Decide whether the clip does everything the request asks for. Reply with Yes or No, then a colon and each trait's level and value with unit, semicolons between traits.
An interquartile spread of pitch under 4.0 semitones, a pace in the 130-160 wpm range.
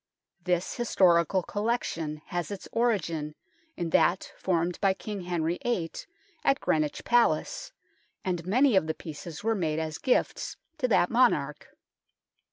No: average, 5.1 semitones; slow, 135 wpm